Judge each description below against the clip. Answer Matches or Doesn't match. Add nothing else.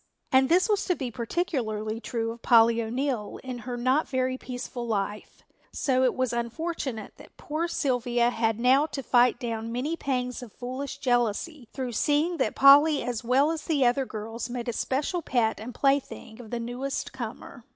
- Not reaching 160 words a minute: Doesn't match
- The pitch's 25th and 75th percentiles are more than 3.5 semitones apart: Doesn't match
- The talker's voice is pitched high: Matches